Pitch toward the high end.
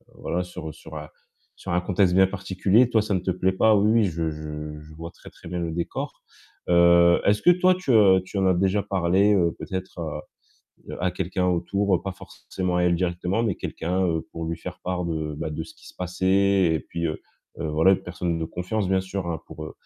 No: very low, 90 Hz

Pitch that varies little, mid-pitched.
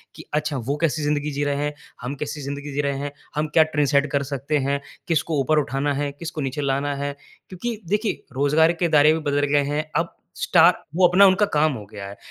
Yes: narrow, 2.0 semitones; medium, 145 Hz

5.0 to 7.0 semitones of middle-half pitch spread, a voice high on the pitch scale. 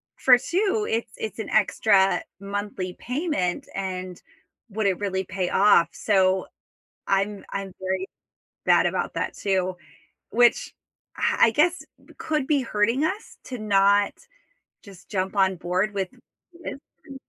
No: average, 4.3 semitones; high, 200 Hz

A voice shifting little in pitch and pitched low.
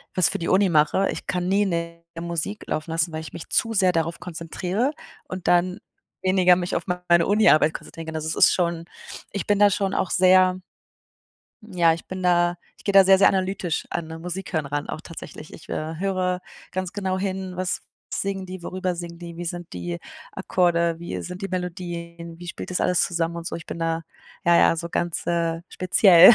No: narrow, 1.9 semitones; medium, 175 Hz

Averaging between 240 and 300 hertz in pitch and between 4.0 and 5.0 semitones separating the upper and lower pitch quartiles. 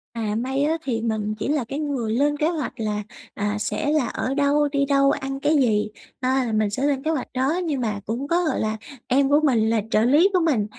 Yes: very high, 270 Hz; average, 4.7 semitones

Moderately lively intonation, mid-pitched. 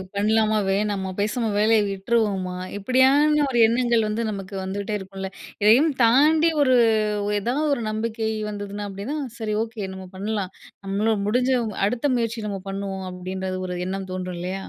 No: average, 3.3 semitones; high, 210 Hz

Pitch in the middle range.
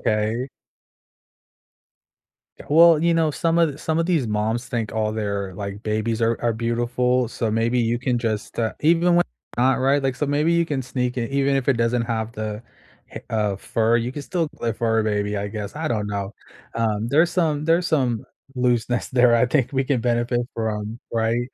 No: low, 120 Hz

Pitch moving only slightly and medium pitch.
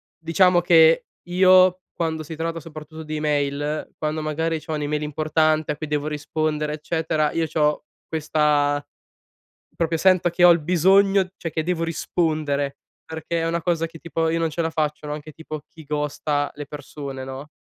Yes: narrow, 1.8 semitones; medium, 155 Hz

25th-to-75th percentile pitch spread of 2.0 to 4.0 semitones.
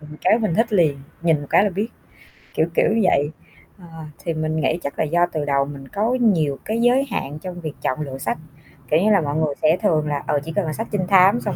No: wide, 5.4 semitones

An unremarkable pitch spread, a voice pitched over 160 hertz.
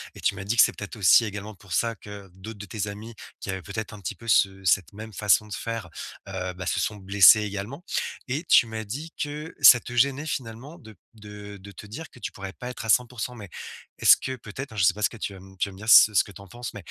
No: average, 3.0 semitones; low, 105 Hz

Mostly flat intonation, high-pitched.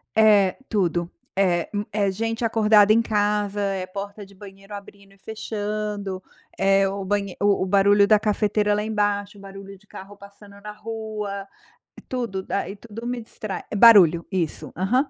Yes: narrow, 1.4 semitones; high, 205 Hz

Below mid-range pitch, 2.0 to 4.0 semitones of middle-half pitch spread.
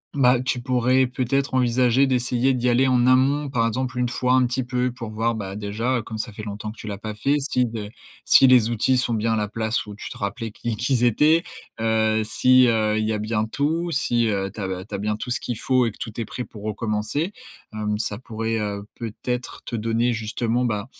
Yes: low, 115 Hz; average, 2.8 semitones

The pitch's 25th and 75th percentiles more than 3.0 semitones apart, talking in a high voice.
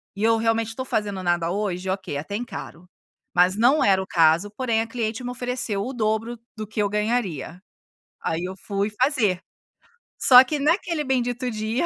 Yes: average, 4.5 semitones; high, 215 Hz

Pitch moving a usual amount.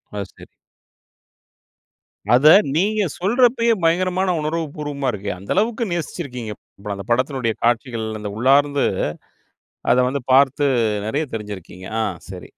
No: wide, 7.2 semitones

